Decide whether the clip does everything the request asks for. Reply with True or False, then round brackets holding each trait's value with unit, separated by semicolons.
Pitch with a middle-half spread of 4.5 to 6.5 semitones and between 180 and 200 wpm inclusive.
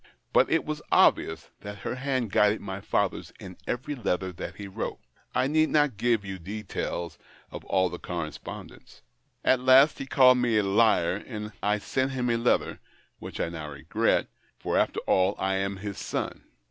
True (5.1 semitones; 185 wpm)